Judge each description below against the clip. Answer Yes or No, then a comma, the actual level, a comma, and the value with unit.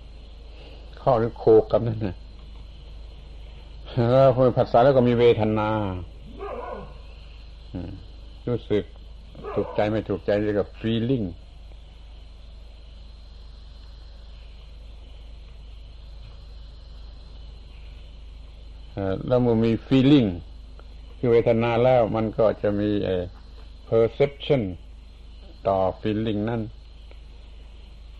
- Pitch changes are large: Yes, wide, 7.1 semitones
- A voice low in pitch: Yes, very low, 75 Hz